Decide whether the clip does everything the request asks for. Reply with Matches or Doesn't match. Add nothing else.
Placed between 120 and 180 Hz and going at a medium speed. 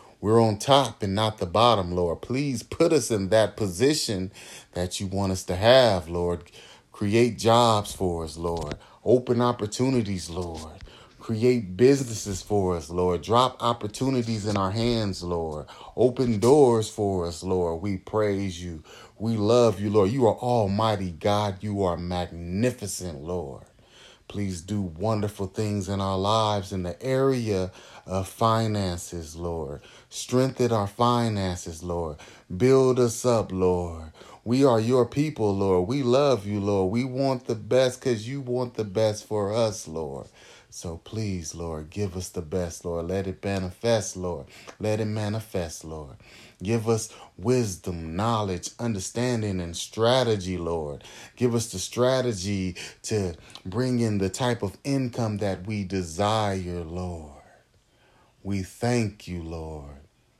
Doesn't match